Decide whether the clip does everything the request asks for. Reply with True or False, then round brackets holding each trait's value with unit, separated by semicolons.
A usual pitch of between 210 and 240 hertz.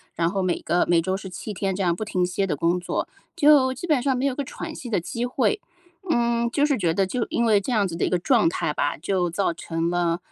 False (195 Hz)